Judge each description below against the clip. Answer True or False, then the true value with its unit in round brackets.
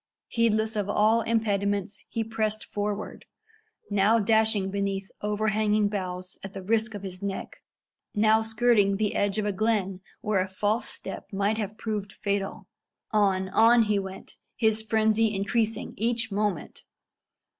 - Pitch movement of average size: False (1.8 semitones)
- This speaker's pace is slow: False (145 wpm)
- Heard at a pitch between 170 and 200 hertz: False (210 Hz)